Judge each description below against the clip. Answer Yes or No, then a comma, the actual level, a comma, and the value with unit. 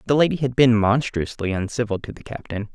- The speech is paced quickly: No, average, 195 wpm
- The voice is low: Yes, low, 115 Hz